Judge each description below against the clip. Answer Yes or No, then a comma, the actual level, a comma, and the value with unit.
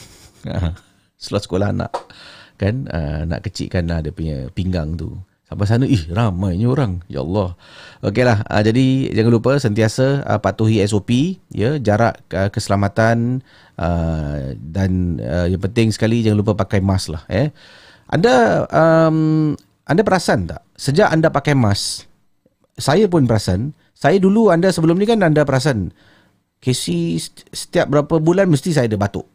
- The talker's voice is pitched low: Yes, low, 105 Hz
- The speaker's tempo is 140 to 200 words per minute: Yes, average, 150 wpm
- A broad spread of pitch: Yes, wide, 6.3 semitones